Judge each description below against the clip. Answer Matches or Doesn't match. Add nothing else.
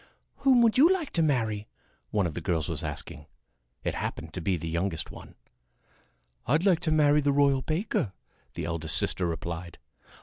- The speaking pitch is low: Matches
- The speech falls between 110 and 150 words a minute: Doesn't match